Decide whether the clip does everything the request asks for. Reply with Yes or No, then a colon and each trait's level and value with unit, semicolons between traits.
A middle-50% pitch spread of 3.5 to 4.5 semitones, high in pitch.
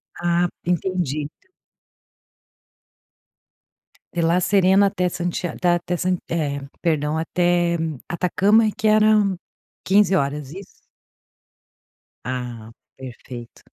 No: average, 4.1 semitones; medium, 175 Hz